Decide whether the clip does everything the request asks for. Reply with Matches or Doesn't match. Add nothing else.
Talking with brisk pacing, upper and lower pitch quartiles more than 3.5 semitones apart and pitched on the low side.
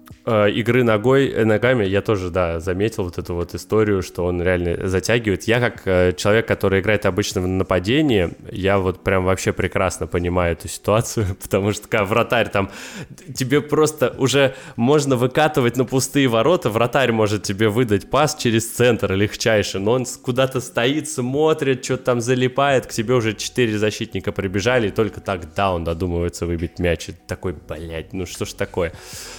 Matches